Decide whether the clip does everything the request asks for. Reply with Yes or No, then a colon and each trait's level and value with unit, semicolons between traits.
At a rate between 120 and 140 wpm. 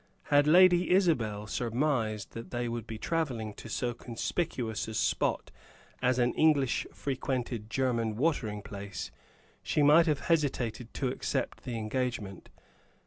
Yes: slow, 135 wpm